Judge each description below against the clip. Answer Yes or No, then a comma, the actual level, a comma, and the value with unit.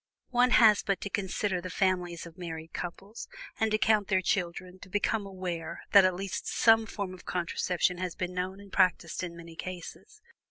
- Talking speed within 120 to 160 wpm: No, average, 190 wpm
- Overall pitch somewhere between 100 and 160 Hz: No, medium, 185 Hz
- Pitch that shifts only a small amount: Yes, narrow, 2.3 semitones